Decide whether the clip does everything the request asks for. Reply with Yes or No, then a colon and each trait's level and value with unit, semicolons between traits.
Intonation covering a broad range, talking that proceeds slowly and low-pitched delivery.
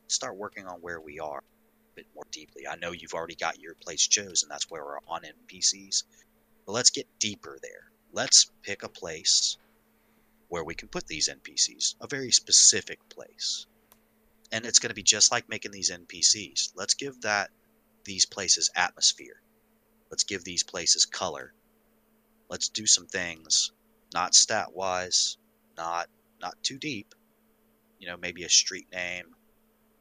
No: wide, 7.7 semitones; average, 160 wpm; very low, 95 Hz